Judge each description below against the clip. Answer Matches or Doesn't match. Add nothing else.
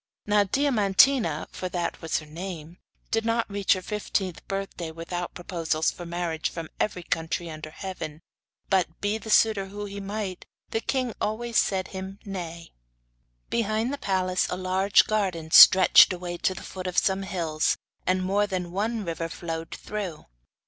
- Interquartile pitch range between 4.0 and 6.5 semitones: Doesn't match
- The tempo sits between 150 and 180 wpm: Matches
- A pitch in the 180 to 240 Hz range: Matches